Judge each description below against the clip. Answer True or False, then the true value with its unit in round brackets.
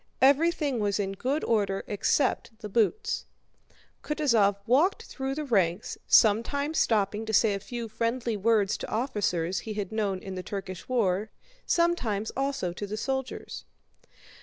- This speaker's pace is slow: False (145 wpm)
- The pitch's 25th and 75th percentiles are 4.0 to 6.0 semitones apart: True (5.0 semitones)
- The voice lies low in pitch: False (220 Hz)